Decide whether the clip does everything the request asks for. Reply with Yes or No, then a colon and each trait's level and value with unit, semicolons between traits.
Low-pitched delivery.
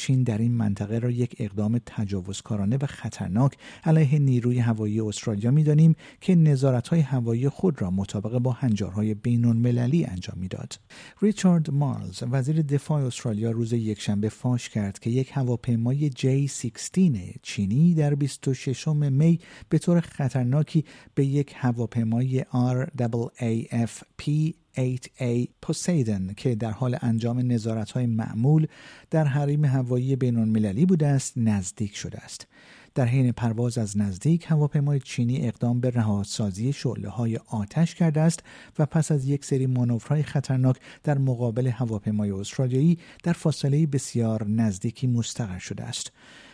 Yes: low, 125 Hz